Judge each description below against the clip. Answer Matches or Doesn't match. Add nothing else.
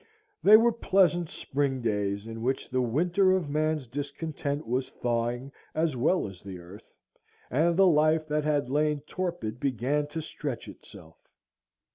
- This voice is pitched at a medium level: Matches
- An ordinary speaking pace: Matches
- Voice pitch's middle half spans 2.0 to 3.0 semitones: Doesn't match